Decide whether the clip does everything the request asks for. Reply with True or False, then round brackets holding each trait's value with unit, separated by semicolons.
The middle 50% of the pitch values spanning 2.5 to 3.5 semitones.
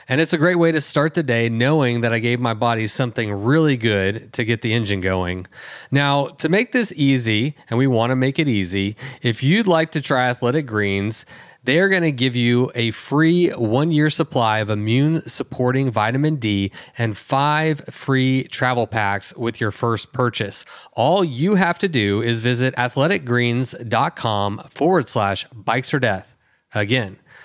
False (4.8 semitones)